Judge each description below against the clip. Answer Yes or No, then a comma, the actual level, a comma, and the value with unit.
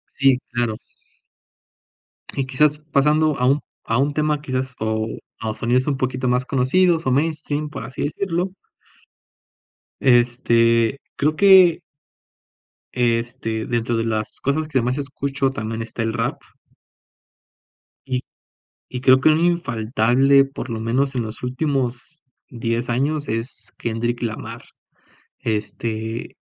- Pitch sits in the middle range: No, low, 130 Hz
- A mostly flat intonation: No, average, 3.8 semitones